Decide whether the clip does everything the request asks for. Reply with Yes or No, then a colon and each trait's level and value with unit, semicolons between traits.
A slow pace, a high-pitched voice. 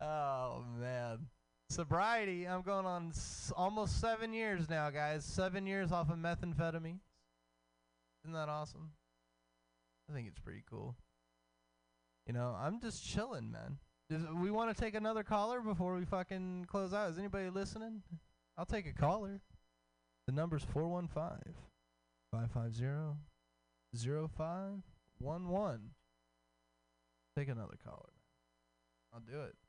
No: slow, 125 wpm; medium, 150 Hz